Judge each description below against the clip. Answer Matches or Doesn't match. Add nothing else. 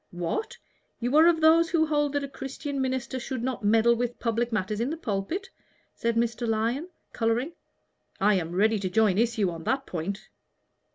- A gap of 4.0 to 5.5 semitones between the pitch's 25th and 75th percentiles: Matches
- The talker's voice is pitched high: Matches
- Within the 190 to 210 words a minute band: Doesn't match